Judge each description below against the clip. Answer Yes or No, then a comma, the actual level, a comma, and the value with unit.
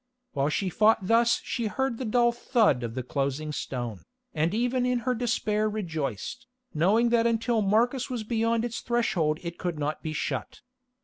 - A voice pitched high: Yes, high, 215 Hz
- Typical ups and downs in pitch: No, wide, 7.4 semitones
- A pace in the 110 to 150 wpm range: No, average, 175 wpm